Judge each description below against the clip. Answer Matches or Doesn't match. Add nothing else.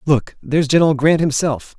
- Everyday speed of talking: Matches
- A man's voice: Matches